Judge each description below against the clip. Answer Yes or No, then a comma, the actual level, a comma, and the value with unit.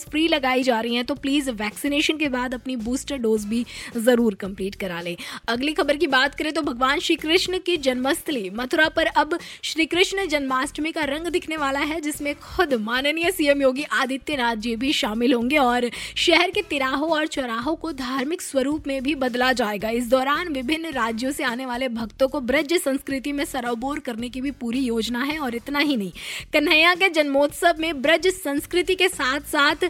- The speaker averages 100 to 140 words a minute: No, fast, 190 wpm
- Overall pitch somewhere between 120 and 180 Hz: No, very high, 280 Hz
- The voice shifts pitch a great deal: No, average, 3.9 semitones